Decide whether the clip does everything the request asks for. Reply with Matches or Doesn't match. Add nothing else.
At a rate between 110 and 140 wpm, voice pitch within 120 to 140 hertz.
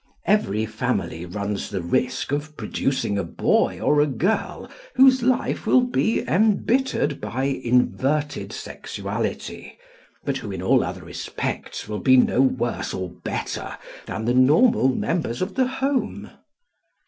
Matches